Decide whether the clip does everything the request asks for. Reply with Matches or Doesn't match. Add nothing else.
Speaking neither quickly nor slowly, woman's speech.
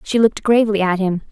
Doesn't match